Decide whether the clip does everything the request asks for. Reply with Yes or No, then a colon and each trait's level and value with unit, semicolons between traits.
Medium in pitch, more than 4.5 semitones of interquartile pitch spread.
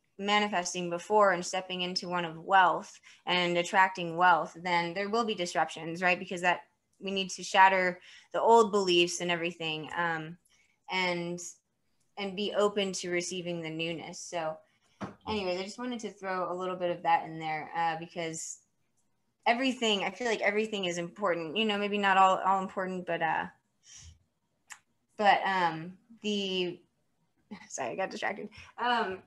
No: medium, 180 Hz; average, 2.7 semitones